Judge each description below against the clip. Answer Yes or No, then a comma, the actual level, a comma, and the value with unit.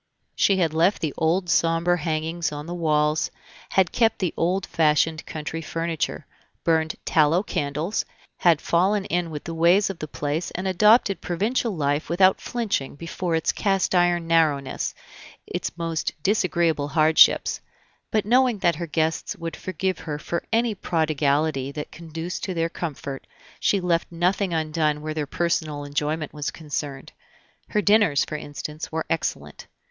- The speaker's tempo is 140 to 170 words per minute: Yes, average, 150 wpm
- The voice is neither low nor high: Yes, medium, 165 Hz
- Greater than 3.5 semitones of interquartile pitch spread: No, average, 2.9 semitones